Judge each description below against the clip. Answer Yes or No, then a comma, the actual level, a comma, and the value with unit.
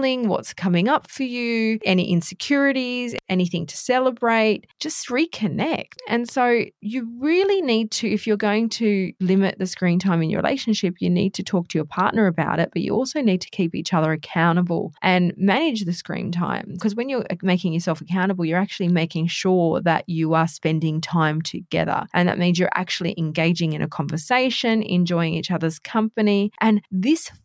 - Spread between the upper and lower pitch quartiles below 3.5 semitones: No, average, 4.7 semitones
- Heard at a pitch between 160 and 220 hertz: Yes, medium, 185 Hz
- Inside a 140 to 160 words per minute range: No, average, 180 wpm